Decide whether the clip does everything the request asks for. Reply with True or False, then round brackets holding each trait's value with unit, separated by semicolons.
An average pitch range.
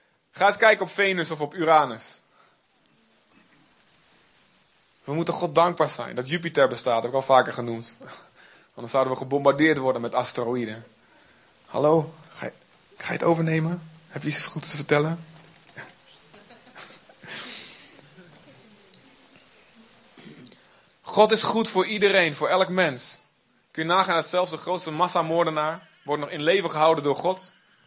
True (3.7 semitones)